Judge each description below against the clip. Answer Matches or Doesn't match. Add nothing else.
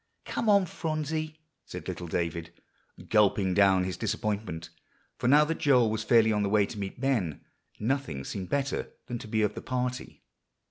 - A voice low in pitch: Matches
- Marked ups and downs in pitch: Matches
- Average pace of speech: Matches